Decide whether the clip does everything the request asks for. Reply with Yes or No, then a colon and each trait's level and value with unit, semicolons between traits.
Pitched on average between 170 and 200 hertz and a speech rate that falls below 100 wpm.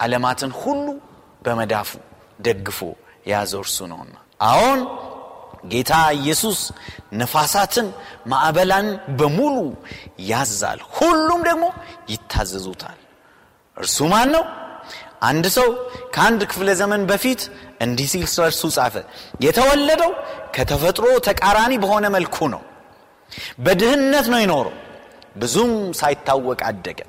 Yes: medium, 185 Hz; average, 90 wpm